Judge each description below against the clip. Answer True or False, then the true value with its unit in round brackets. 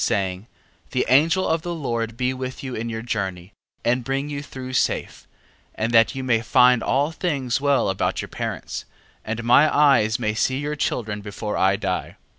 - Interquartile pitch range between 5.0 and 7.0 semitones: False (4.0 semitones)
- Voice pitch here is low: True (125 Hz)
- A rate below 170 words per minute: False (190 wpm)